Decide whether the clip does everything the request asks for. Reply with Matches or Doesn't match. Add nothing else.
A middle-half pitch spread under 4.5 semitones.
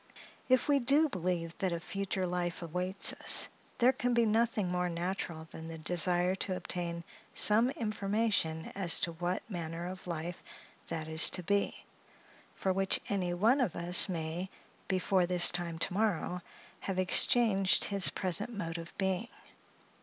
Matches